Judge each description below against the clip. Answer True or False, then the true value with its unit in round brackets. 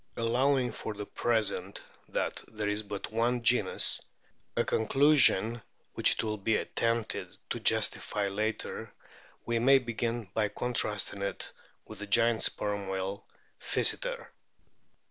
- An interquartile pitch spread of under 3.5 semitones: True (2.5 semitones)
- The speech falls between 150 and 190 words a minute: False (135 wpm)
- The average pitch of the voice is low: True (110 Hz)